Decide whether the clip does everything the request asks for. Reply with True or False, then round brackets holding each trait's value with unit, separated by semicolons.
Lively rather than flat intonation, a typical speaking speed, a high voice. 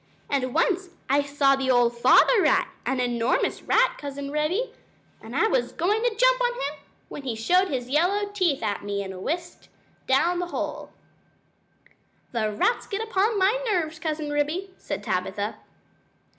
True (7.0 semitones; 165 wpm; 310 Hz)